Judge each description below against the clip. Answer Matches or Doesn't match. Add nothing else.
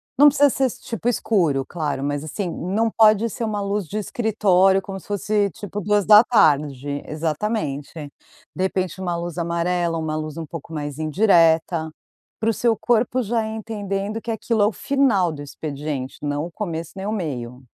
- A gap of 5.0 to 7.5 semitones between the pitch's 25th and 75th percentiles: Matches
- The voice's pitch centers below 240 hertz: Matches